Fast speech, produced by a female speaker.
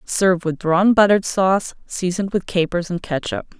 No: average, 165 wpm; female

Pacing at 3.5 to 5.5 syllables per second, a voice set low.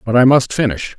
No: 5.8 syllables/s; low, 125 Hz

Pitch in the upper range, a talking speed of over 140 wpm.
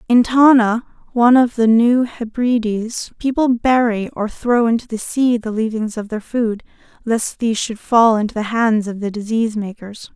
Yes: high, 230 Hz; average, 175 wpm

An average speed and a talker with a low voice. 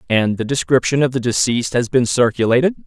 Yes: average, 190 wpm; low, 125 Hz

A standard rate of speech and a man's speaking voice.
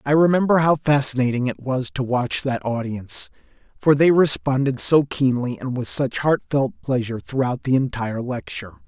Yes: average, 160 wpm; male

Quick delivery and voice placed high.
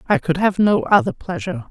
Yes: fast, 210 wpm; high, 195 Hz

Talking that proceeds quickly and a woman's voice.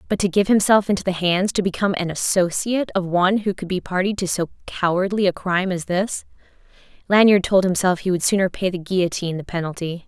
Yes: fast, 210 wpm; female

